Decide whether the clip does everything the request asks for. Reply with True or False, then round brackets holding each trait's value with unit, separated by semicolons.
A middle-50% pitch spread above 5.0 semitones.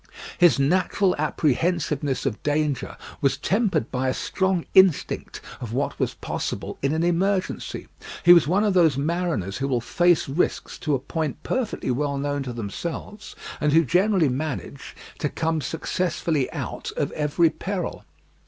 False (4.3 semitones)